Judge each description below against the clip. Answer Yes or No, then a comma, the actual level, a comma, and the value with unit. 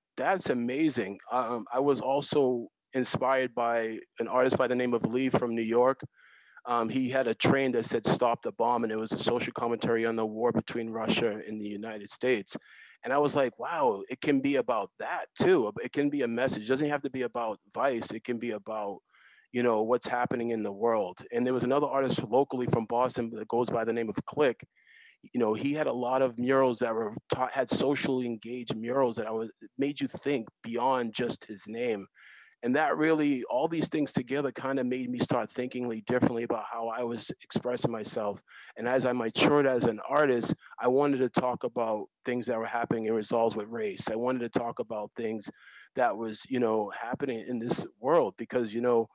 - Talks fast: Yes, fast, 210 wpm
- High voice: No, low, 125 Hz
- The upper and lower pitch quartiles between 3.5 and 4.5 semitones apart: No, narrow, 2.4 semitones